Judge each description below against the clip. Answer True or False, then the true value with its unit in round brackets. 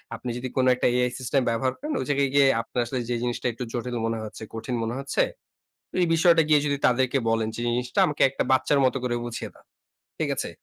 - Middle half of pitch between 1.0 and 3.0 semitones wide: True (2.5 semitones)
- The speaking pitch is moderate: False (125 Hz)